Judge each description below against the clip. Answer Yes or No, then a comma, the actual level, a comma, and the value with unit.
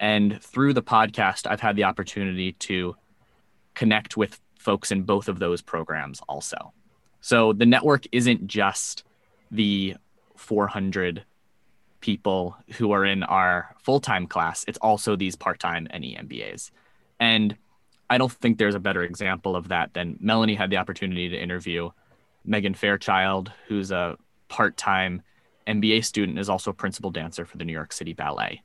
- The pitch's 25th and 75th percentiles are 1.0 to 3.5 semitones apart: Yes, average, 2.7 semitones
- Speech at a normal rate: Yes, average, 155 wpm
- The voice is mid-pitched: No, low, 100 Hz